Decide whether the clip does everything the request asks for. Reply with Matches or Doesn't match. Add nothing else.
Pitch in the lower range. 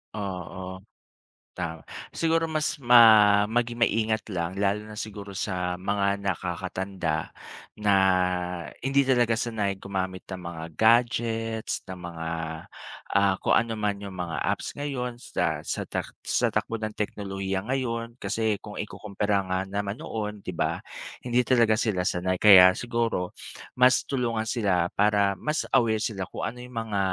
Matches